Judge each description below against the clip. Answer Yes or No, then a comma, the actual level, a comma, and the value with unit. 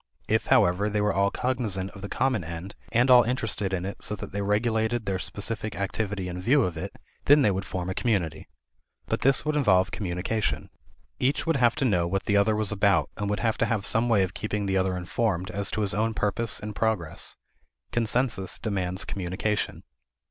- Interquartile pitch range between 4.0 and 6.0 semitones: No, average, 3.1 semitones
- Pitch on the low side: Yes, low, 105 Hz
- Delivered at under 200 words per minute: No, fast, 205 wpm